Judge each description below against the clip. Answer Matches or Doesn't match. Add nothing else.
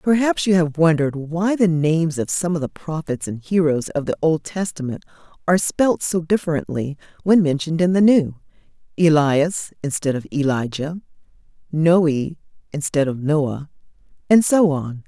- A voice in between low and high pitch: Matches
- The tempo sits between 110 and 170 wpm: Matches